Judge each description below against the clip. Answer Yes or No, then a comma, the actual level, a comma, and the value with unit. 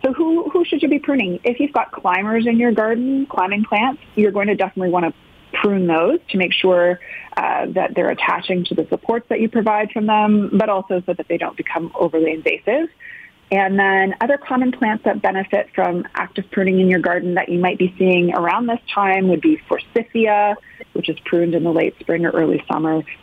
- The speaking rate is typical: No, fast, 210 wpm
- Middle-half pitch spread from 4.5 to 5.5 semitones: Yes, average, 4.9 semitones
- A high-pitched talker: Yes, high, 200 Hz